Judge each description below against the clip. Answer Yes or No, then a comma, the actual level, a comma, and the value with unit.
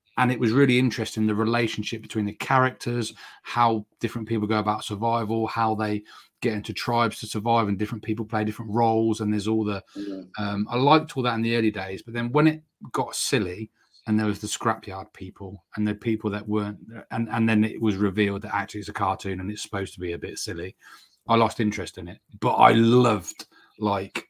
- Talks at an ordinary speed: No, fast, 215 wpm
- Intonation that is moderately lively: No, narrow, 1.9 semitones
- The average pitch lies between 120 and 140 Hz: No, low, 110 Hz